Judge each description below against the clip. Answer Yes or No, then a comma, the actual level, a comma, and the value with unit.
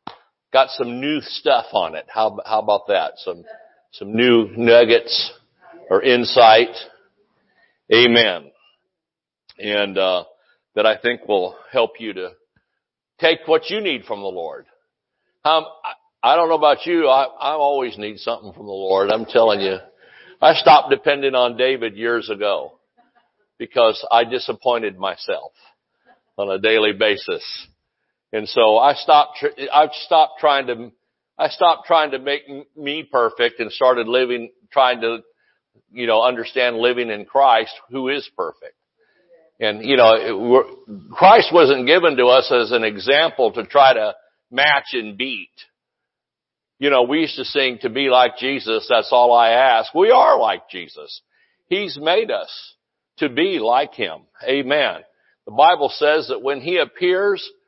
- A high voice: No, low, 135 Hz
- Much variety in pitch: Yes, wide, 6.1 semitones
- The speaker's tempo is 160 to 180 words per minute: No, average, 150 wpm